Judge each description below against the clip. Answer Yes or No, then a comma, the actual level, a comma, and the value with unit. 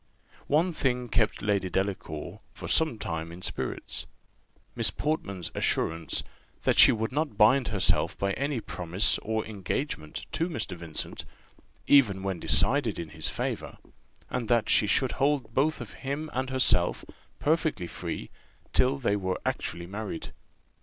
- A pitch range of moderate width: No, wide, 6.7 semitones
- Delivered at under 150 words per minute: Yes, average, 140 wpm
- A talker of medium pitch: No, low, 110 Hz